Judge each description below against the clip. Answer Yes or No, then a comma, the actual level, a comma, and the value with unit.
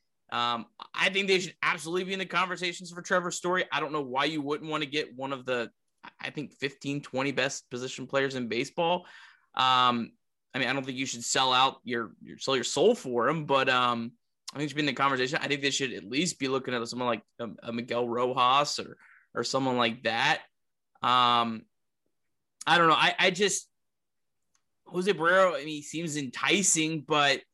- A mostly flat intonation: No, average, 4.4 semitones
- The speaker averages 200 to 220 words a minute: Yes, fast, 205 wpm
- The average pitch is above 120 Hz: Yes, medium, 140 Hz